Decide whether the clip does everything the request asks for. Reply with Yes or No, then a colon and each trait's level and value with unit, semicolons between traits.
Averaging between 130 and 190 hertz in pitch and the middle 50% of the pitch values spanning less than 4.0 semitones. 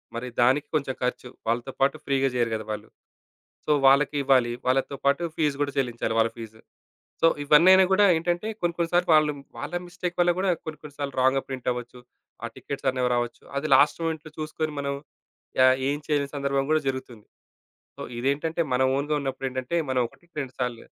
Yes: medium, 140 Hz; average, 3.5 semitones